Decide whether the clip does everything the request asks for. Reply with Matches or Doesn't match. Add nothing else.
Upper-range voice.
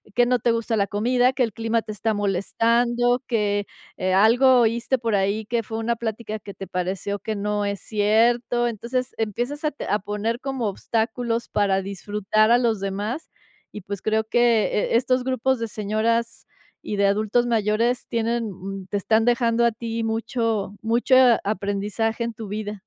Matches